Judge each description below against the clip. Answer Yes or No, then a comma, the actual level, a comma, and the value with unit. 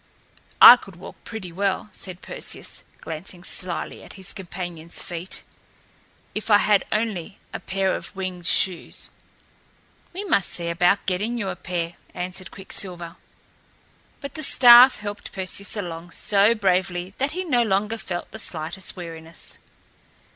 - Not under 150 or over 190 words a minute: No, average, 140 wpm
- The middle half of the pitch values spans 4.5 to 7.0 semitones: No, average, 3.2 semitones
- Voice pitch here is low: No, high, 190 Hz